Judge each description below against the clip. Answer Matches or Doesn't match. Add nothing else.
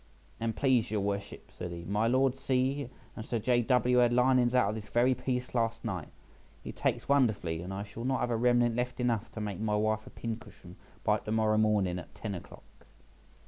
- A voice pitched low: Matches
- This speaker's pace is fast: Matches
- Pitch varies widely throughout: Doesn't match